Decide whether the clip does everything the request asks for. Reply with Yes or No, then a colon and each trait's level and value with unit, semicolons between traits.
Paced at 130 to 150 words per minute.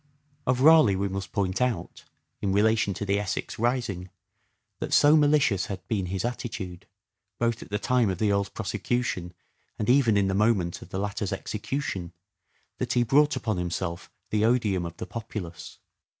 No: average, 170 wpm